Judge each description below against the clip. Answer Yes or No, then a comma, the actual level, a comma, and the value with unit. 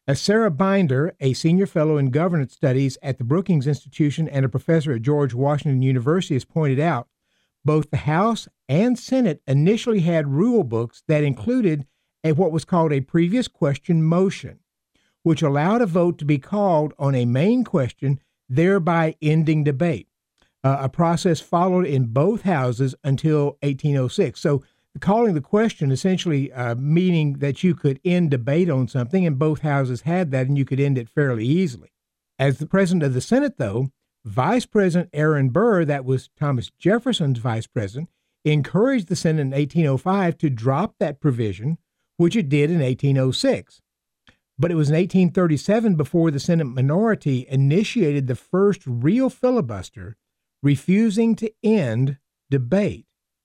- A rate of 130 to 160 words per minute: Yes, average, 155 wpm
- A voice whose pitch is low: No, medium, 155 Hz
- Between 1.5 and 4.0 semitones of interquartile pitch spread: No, average, 5.0 semitones